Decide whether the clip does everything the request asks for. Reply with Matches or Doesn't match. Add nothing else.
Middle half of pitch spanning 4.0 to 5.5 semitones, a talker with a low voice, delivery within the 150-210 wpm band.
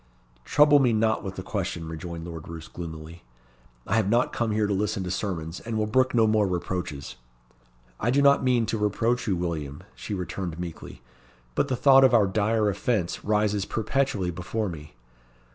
Matches